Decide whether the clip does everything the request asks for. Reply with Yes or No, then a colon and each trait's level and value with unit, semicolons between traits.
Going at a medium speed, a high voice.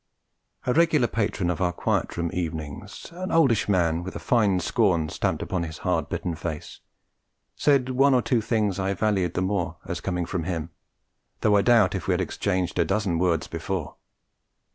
No: average, 185 wpm; very low, 95 Hz